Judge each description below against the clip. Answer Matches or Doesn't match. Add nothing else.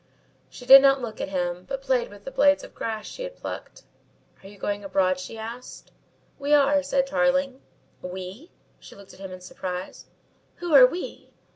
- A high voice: Matches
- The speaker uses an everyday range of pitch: Doesn't match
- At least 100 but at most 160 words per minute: Doesn't match